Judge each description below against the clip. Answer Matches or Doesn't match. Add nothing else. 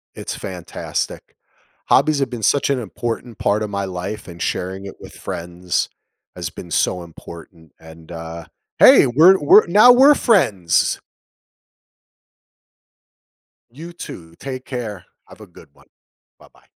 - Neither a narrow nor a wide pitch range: Doesn't match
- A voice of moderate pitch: Doesn't match